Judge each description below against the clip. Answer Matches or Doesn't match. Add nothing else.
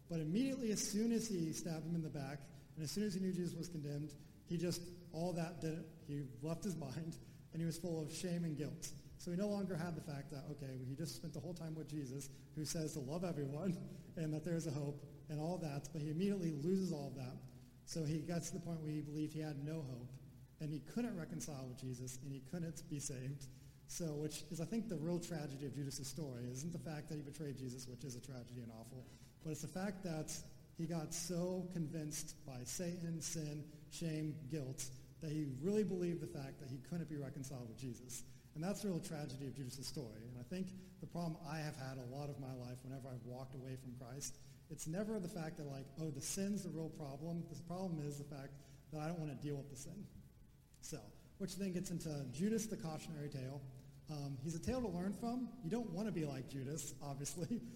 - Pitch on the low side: Doesn't match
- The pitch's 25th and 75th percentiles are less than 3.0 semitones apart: Doesn't match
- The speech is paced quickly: Matches